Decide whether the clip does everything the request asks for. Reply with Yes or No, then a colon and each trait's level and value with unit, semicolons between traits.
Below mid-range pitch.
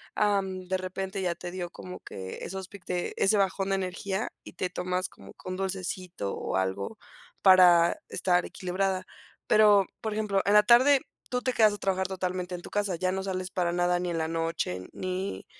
No: medium, 185 Hz